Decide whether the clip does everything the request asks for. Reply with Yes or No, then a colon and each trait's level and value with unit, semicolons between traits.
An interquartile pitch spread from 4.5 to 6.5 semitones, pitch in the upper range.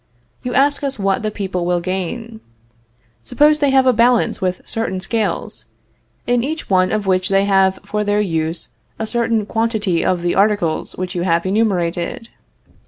No: average, 3.8 semitones; high, 205 Hz